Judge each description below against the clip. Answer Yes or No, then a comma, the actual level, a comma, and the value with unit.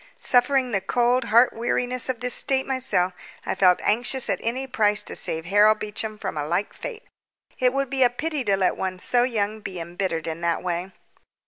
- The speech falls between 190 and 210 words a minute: Yes, average, 200 wpm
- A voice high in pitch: Yes, high, 220 Hz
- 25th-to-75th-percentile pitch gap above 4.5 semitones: Yes, average, 5.0 semitones